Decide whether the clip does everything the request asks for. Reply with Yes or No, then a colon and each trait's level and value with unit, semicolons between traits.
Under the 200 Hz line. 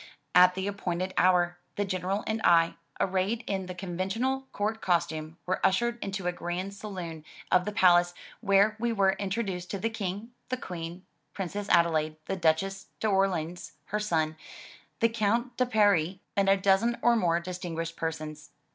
Yes: high, 190 Hz